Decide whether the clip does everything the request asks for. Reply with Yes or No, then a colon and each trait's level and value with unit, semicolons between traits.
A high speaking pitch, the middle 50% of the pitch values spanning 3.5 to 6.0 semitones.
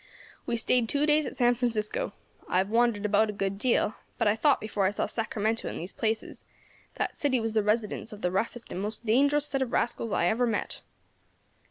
No: high, 225 Hz; narrow, 2.6 semitones